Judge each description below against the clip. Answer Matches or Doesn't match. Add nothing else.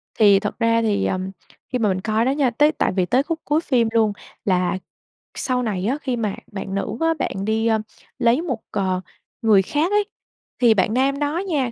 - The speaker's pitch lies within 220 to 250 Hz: Matches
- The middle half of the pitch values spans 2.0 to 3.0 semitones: Doesn't match